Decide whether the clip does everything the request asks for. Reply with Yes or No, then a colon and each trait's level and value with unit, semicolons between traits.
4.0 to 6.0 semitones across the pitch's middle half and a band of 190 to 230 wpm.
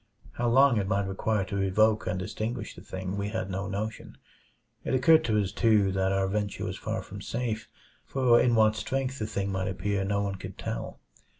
No: average, 2.8 semitones; fast, 205 wpm